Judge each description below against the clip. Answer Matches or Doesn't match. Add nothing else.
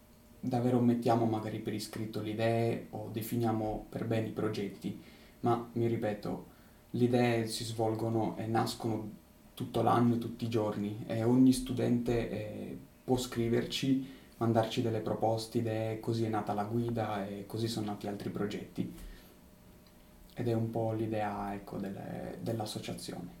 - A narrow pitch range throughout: Matches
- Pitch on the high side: Doesn't match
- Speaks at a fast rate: Doesn't match